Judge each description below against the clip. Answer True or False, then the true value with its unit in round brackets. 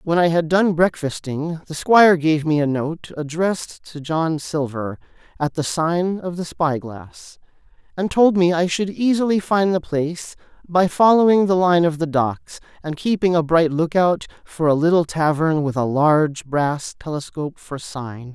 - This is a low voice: False (165 Hz)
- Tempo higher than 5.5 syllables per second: False (4.5 syllables/s)